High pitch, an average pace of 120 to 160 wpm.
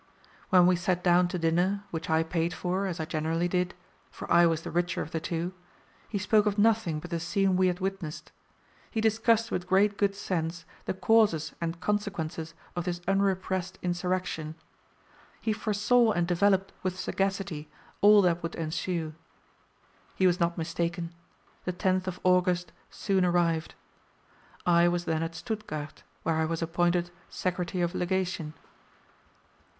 No: medium, 180 Hz; average, 155 wpm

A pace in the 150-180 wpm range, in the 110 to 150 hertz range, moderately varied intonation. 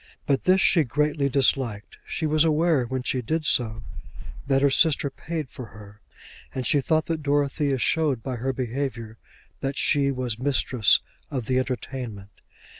Yes: average, 160 wpm; low, 135 Hz; average, 3.3 semitones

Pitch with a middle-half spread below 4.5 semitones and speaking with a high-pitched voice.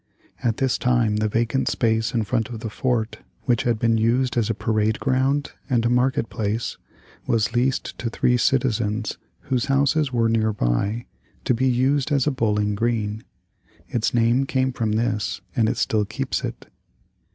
No: average, 2.8 semitones; low, 115 Hz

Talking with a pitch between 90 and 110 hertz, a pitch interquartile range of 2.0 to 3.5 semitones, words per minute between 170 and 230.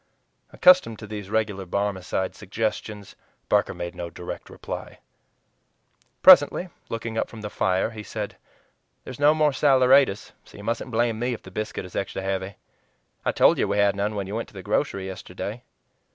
Yes: low, 105 Hz; average, 3.2 semitones; average, 175 wpm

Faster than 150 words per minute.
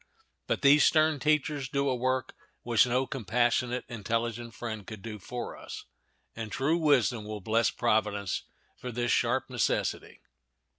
No: average, 145 wpm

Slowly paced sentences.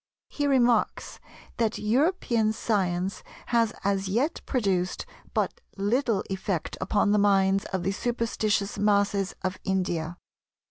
Yes: slow, 120 wpm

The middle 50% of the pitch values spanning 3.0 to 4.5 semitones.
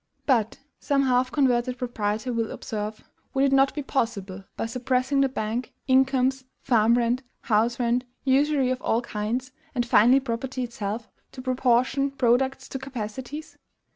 No: narrow, 2.5 semitones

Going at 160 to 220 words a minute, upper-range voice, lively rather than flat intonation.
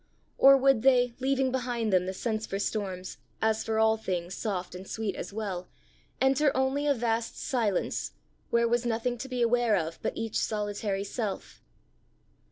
No: average, 170 wpm; high, 225 Hz; average, 3.7 semitones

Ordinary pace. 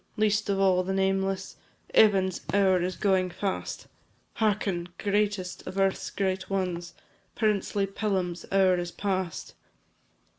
No: slow, 120 wpm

